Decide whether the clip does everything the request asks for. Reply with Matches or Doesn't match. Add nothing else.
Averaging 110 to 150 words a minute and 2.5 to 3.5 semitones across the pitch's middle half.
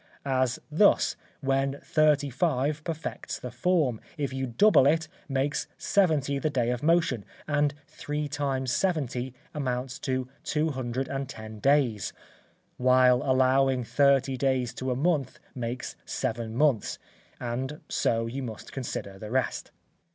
Matches